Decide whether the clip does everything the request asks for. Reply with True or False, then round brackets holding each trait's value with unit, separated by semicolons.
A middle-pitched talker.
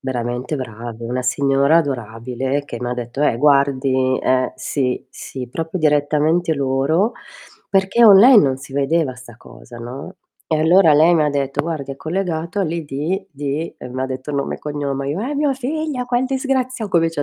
True (145 Hz)